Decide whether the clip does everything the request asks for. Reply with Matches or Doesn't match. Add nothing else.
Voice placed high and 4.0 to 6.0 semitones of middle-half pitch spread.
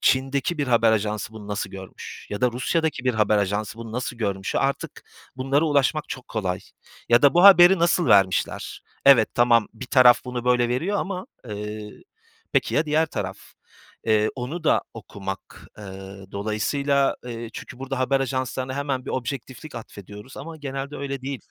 Doesn't match